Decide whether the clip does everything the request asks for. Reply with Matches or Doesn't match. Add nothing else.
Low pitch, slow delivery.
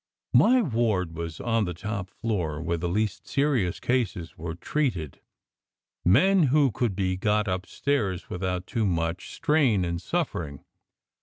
Doesn't match